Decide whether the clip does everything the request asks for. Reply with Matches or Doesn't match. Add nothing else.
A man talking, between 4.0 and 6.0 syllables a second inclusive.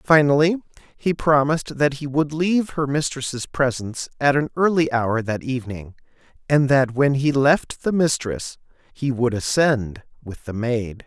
Matches